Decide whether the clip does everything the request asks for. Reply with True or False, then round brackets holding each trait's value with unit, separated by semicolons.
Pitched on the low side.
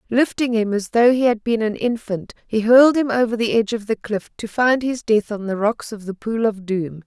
False (225 Hz)